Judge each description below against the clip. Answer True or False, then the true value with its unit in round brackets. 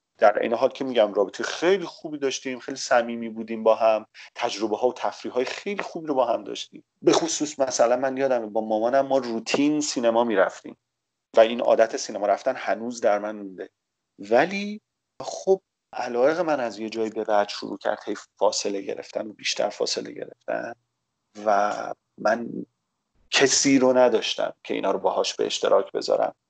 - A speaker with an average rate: False (170 wpm)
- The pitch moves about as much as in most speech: True (3.9 semitones)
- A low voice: True (125 Hz)